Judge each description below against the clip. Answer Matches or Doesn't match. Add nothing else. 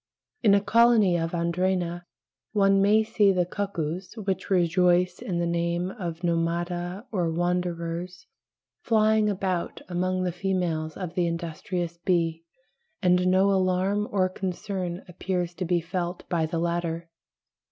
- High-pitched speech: Doesn't match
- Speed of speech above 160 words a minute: Doesn't match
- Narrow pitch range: Matches